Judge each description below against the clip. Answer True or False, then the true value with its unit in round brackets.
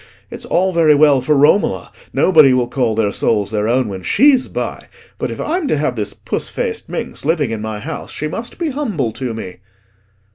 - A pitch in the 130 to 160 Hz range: True (135 Hz)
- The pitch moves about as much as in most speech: False (7.2 semitones)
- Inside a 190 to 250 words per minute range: True (195 wpm)